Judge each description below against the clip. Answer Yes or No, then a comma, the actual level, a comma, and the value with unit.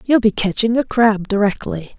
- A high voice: Yes, high, 215 Hz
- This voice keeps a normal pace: Yes, average, 180 wpm